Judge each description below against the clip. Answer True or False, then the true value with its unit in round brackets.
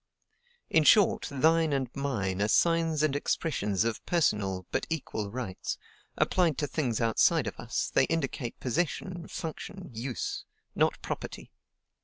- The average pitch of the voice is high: False (140 Hz)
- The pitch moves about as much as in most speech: False (6.3 semitones)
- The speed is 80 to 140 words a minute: True (135 wpm)